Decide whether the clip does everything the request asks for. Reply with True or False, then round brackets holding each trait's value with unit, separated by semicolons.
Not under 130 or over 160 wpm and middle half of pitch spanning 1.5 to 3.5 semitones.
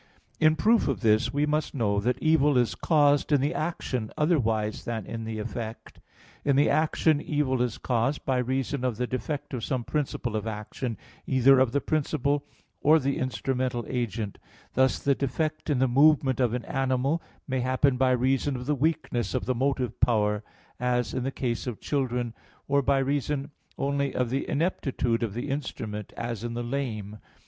False (180 wpm; 3.1 semitones)